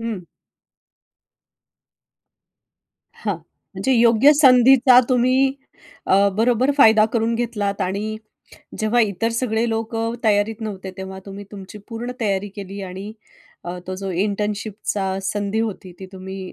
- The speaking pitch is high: Yes, high, 215 Hz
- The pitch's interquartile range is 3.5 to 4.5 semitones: No, average, 3.0 semitones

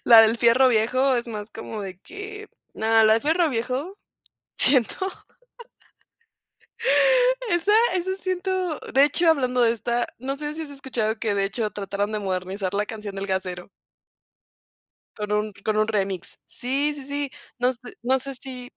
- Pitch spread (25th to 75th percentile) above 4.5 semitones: Yes, average, 5.2 semitones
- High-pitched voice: Yes, high, 240 Hz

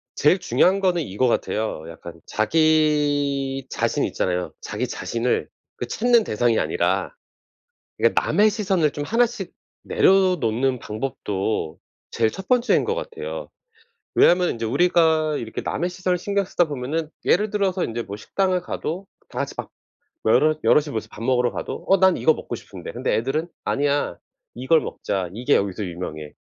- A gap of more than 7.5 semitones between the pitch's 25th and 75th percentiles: Yes, wide, 8.1 semitones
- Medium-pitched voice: Yes, medium, 150 Hz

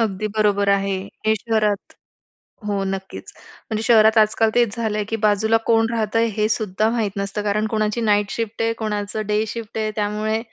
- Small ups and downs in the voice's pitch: Yes, narrow, 1.4 semitones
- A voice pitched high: Yes, high, 215 Hz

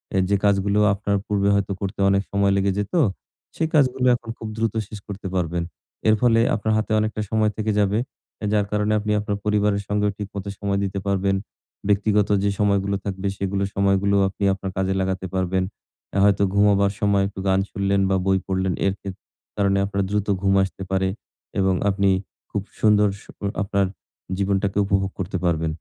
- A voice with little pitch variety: Yes, narrow, 1.1 semitones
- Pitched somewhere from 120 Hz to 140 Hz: No, low, 100 Hz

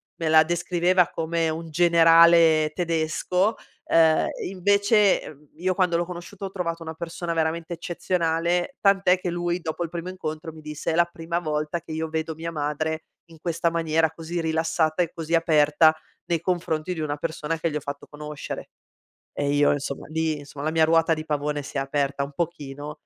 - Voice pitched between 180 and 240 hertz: No, medium, 165 Hz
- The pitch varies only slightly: Yes, narrow, 1.8 semitones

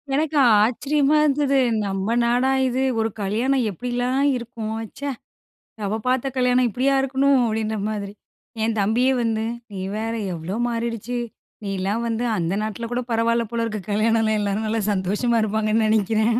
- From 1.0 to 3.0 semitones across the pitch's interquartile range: Yes, average, 2.7 semitones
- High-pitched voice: Yes, high, 230 Hz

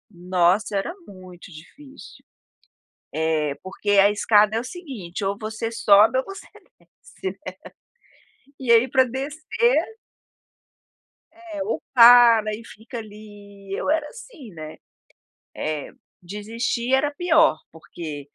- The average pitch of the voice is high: Yes, high, 215 Hz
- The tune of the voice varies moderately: No, wide, 5.7 semitones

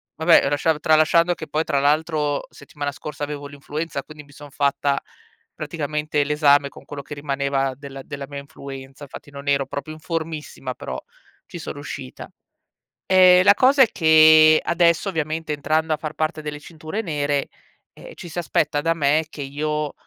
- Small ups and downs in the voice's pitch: Yes, narrow, 1.9 semitones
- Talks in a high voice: No, medium, 150 Hz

